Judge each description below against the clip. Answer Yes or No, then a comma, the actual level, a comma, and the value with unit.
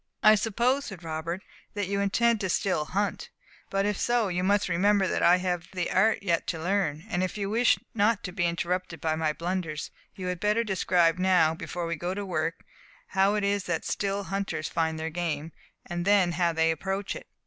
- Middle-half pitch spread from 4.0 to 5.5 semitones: No, average, 3.1 semitones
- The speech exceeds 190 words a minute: Yes, fast, 205 wpm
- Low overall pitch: No, medium, 185 Hz